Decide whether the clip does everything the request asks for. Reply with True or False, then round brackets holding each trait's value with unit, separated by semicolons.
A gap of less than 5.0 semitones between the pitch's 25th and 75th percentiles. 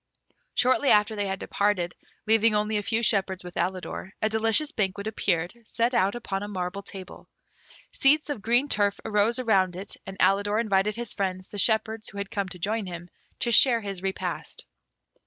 True (2.8 semitones)